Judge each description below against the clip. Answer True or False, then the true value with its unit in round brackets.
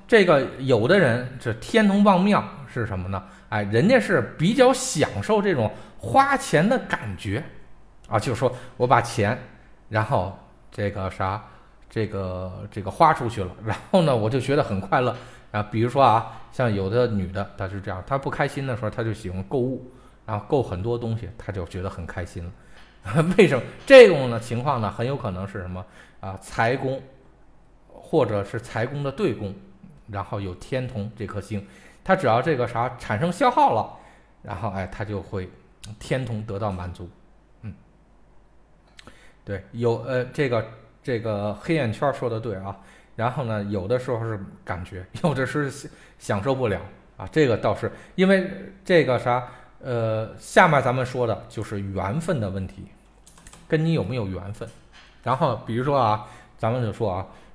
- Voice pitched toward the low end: True (115 Hz)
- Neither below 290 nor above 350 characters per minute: False (245 characters per minute)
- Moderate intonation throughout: True (4.7 semitones)